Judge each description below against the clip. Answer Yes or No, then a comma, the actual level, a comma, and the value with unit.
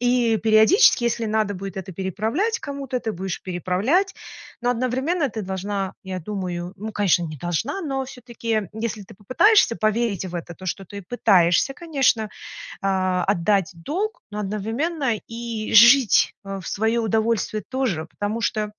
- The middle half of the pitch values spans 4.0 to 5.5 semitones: Yes, average, 4.4 semitones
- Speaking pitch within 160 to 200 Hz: No, high, 215 Hz